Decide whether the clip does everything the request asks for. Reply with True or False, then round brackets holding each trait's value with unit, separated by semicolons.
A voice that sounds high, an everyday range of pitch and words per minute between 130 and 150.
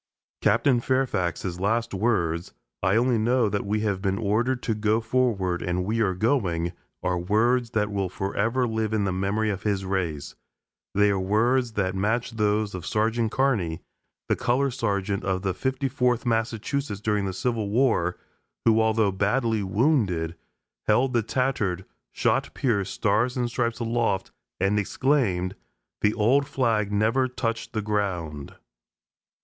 False (110 Hz; 3.6 semitones; 145 wpm)